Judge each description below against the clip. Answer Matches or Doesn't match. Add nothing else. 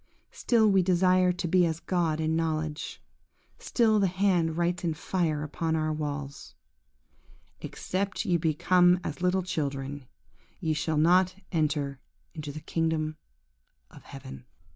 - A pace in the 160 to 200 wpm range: Doesn't match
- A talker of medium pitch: Matches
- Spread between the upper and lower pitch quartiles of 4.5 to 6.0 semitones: Doesn't match